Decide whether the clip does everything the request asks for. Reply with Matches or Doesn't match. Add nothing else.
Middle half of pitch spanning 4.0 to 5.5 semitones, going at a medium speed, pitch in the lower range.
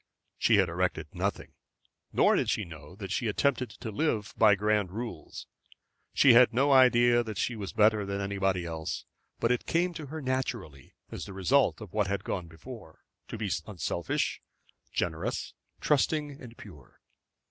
Matches